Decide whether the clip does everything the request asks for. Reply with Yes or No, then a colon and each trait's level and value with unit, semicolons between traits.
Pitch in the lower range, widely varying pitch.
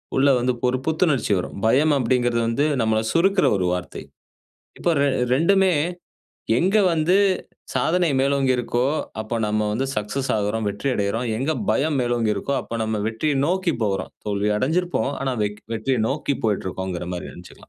Yes: low, 125 Hz; wide, 5.9 semitones